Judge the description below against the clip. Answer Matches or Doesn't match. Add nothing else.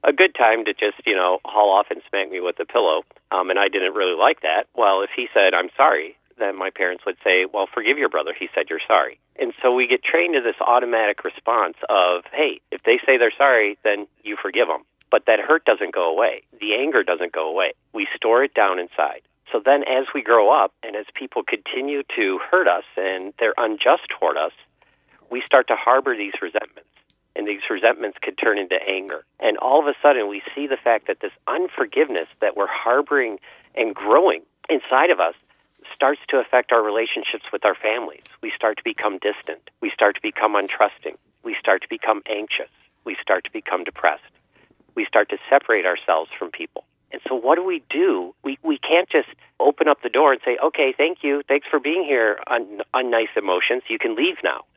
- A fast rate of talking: Matches